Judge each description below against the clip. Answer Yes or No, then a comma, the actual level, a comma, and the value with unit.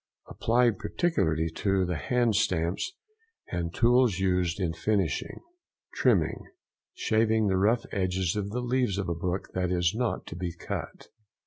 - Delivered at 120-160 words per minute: Yes, average, 140 wpm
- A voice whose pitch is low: Yes, very low, 95 Hz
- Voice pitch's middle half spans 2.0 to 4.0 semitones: No, average, 4.6 semitones